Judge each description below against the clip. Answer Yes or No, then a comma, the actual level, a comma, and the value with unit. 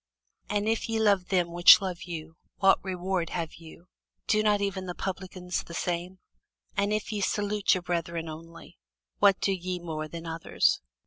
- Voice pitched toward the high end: No, medium, 180 Hz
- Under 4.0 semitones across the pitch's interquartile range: Yes, average, 2.9 semitones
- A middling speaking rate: Yes, average, 175 wpm